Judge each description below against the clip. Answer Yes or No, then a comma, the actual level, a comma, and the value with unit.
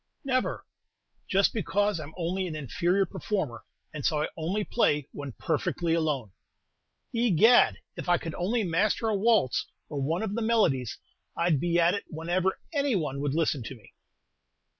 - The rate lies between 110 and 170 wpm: Yes, average, 160 wpm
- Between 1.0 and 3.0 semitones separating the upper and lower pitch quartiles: No, average, 5.3 semitones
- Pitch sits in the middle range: Yes, medium, 175 Hz